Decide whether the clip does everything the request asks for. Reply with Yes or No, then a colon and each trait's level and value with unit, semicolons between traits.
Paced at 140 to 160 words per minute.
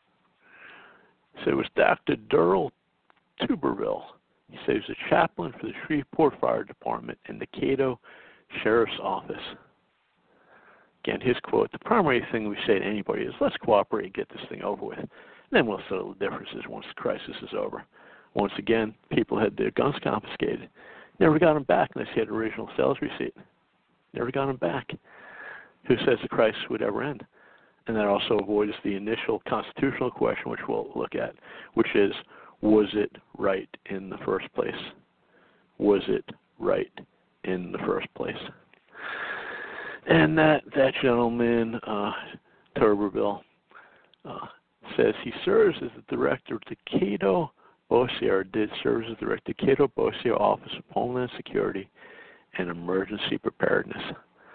Yes: average, 155 wpm